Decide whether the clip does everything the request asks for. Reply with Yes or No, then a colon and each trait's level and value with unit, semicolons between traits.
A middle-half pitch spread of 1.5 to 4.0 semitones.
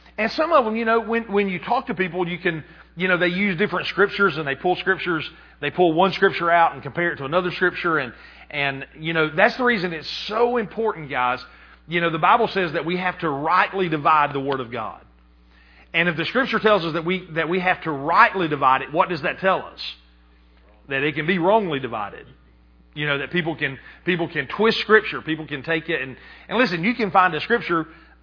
No: average, 5.3 semitones